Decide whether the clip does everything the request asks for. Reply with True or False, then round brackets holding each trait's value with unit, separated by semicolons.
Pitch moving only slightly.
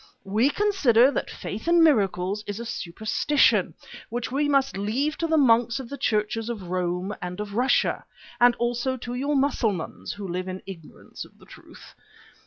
False (5.4 semitones)